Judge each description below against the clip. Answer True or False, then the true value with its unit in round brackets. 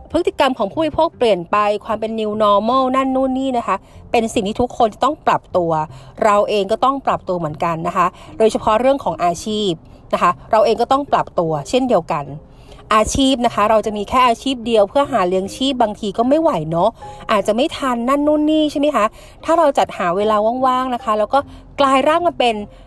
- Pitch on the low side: False (230 Hz)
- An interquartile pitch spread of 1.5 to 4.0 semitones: False (4.7 semitones)